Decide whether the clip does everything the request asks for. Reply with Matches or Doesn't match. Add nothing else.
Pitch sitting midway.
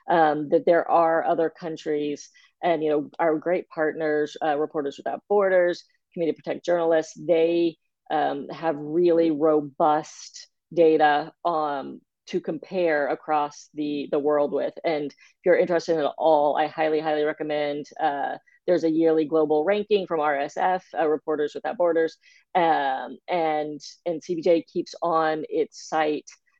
Matches